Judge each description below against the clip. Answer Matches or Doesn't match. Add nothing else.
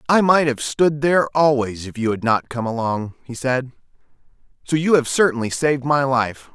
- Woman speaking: Doesn't match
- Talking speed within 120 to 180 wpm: Doesn't match